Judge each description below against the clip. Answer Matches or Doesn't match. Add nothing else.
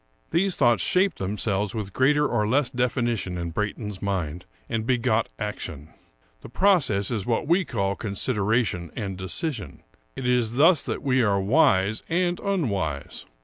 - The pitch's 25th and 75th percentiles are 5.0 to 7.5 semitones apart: Matches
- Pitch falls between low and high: Doesn't match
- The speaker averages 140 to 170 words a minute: Matches